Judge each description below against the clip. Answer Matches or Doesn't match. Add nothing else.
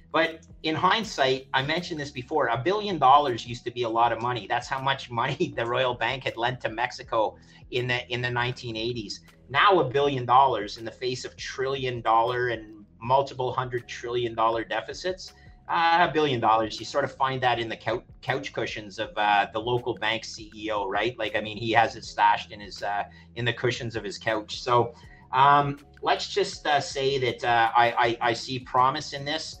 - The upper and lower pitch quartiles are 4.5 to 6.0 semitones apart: Doesn't match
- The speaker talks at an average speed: Doesn't match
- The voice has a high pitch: Doesn't match